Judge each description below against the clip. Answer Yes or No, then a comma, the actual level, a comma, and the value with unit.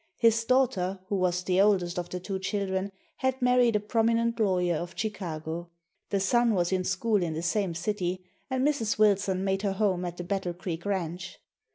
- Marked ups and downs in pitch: No, average, 3.4 semitones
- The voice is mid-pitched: No, high, 195 Hz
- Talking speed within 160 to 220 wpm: Yes, average, 190 wpm